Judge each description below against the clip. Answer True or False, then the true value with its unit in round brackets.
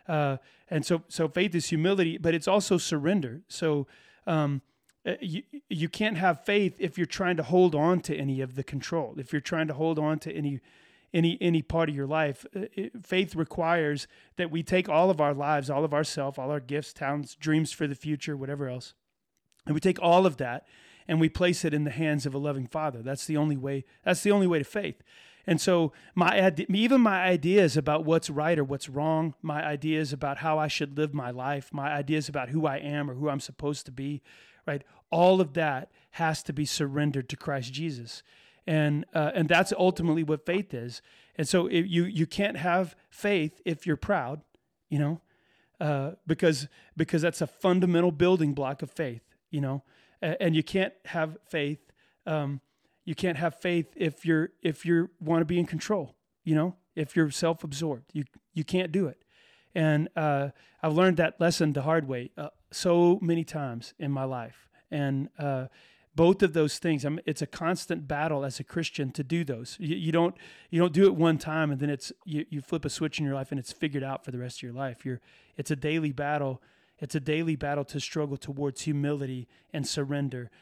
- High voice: False (155 Hz)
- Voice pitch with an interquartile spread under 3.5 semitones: True (2.9 semitones)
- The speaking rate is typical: False (210 wpm)